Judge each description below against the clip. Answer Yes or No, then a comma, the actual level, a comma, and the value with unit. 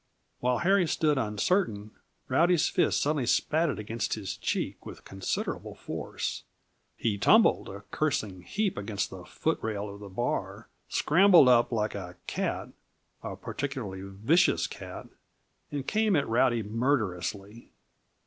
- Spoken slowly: Yes, slow, 130 wpm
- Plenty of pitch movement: Yes, wide, 6.9 semitones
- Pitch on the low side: Yes, low, 120 Hz